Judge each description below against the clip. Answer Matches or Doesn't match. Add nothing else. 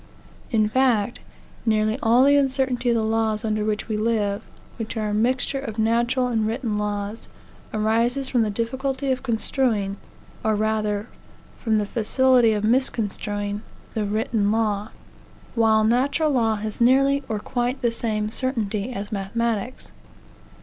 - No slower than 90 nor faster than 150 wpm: Matches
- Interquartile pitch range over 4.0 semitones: Doesn't match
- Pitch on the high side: Matches